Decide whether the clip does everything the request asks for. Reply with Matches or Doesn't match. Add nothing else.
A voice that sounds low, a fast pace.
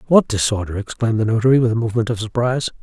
Matches